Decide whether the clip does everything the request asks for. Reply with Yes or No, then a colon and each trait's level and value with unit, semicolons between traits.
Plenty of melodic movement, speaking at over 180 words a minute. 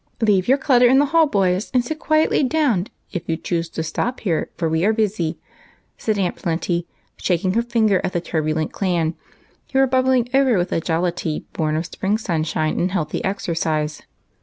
Yes: wide, 6.6 semitones; average, 190 wpm